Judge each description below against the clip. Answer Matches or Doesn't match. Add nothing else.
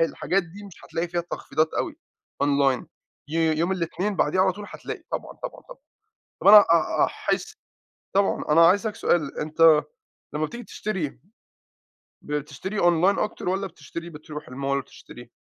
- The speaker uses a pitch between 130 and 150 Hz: Doesn't match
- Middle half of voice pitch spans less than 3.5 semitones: Doesn't match